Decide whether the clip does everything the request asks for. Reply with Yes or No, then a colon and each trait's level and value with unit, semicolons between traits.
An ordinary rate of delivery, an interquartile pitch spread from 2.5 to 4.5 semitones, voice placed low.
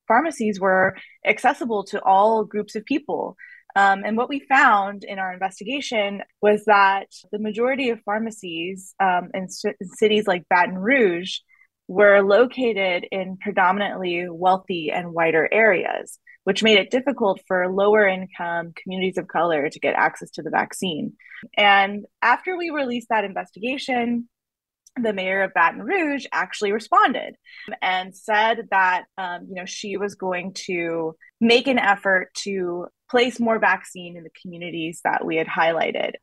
No: average, 150 wpm; average, 3.4 semitones; high, 200 Hz